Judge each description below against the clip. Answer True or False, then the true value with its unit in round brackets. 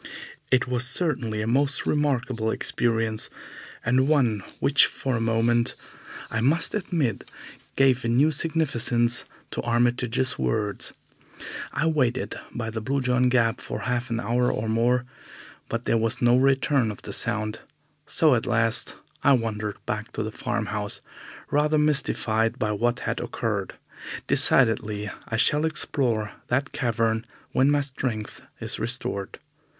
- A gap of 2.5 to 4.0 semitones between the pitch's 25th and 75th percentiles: True (3.1 semitones)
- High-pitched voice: False (120 Hz)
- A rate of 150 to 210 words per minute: False (140 wpm)